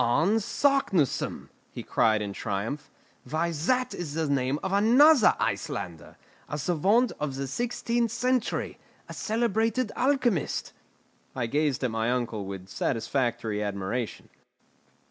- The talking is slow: Yes, slow, 125 wpm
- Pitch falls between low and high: Yes, medium, 150 Hz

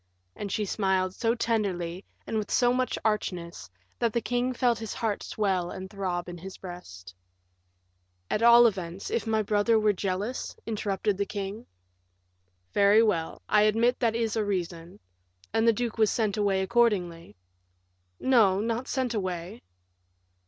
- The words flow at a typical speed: Yes, average, 150 wpm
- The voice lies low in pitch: No, high, 210 Hz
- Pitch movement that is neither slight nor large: Yes, average, 3.5 semitones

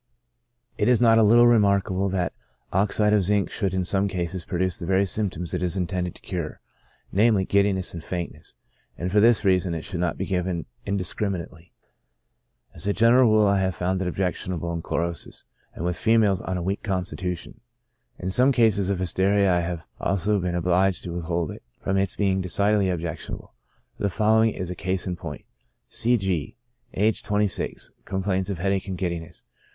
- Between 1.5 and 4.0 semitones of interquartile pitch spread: Yes, narrow, 2.4 semitones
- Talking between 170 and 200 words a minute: Yes, average, 180 wpm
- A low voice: Yes, very low, 95 Hz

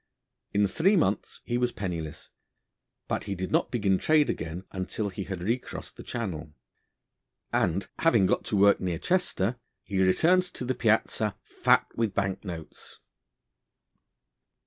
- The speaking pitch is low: Yes, low, 100 Hz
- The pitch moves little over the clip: No, average, 4.4 semitones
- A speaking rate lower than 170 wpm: Yes, average, 145 wpm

